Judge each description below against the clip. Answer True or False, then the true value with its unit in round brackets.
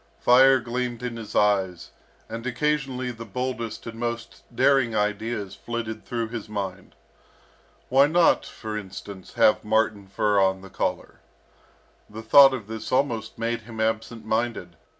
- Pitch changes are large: False (2.7 semitones)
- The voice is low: True (115 Hz)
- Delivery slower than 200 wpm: True (145 wpm)